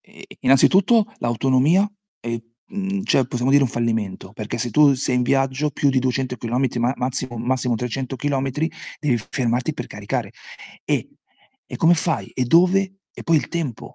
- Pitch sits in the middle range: No, low, 130 Hz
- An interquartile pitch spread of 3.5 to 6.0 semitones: Yes, average, 3.9 semitones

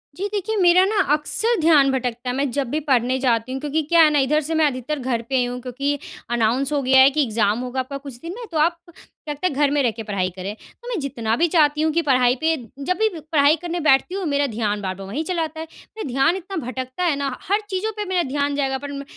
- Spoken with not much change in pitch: No, average, 4.3 semitones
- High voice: Yes, very high, 285 Hz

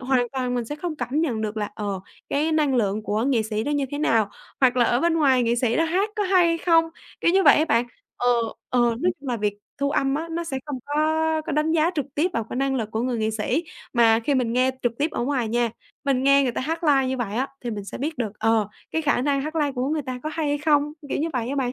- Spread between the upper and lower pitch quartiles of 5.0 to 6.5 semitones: No, average, 4.3 semitones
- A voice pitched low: No, very high, 265 Hz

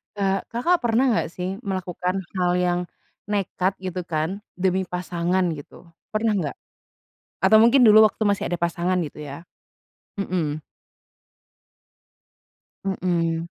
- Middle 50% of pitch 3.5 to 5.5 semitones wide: No, average, 2.9 semitones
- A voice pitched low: No, medium, 185 Hz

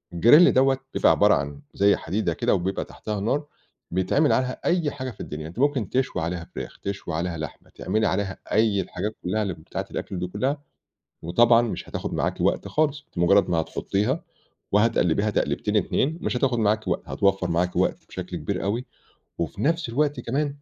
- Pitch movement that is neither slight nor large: No, wide, 6.5 semitones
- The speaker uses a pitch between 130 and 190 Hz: No, low, 105 Hz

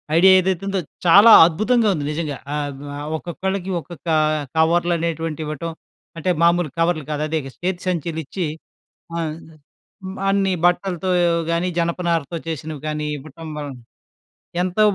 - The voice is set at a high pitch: No, medium, 170 Hz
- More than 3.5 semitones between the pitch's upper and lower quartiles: No, average, 2.9 semitones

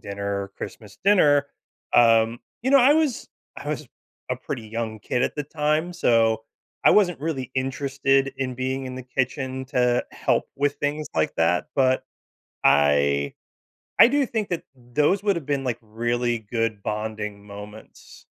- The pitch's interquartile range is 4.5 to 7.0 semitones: Yes, average, 4.8 semitones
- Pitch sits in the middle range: No, low, 130 Hz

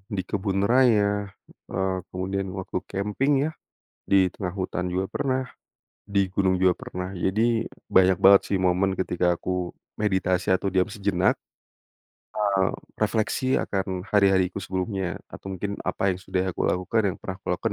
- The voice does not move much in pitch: Yes, narrow, 1.6 semitones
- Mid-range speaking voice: No, very low, 95 Hz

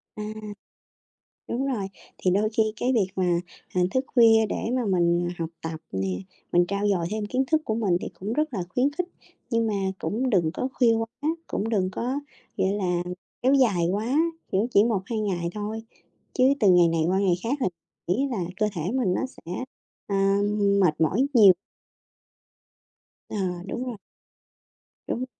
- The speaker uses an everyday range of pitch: Yes, average, 4.7 semitones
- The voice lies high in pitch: Yes, high, 210 Hz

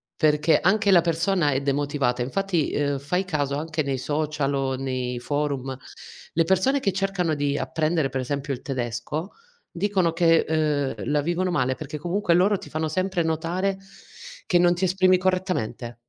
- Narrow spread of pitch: No, average, 4.5 semitones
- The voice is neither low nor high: Yes, medium, 155 Hz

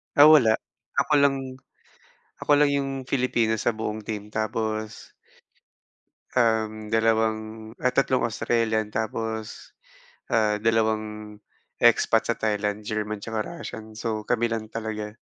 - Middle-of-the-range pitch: No, low, 110 Hz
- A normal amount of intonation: No, narrow, 1.3 semitones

